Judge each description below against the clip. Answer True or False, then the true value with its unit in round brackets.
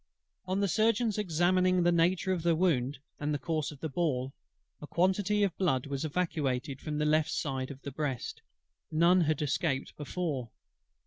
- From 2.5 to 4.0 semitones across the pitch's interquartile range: False (4.4 semitones)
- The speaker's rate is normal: True (175 wpm)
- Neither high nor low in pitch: True (160 Hz)